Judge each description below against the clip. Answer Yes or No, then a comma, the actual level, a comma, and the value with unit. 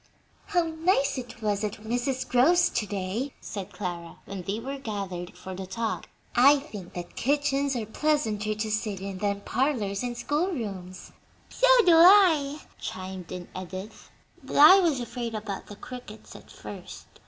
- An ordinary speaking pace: Yes, average, 165 wpm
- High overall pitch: Yes, high, 225 Hz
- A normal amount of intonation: No, wide, 6.1 semitones